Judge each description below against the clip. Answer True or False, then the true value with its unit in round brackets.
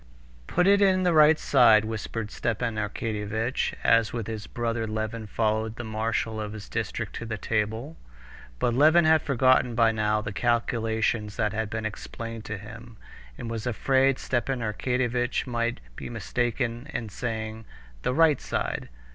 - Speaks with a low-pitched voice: True (115 Hz)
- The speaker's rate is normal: True (155 wpm)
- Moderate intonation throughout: False (2.3 semitones)